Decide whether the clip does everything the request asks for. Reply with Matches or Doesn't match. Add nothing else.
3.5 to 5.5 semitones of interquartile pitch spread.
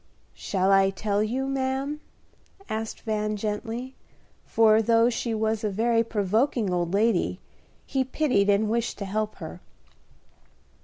Doesn't match